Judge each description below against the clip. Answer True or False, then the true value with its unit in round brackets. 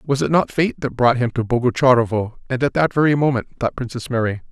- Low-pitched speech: True (125 Hz)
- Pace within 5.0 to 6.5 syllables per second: True (6.0 syllables/s)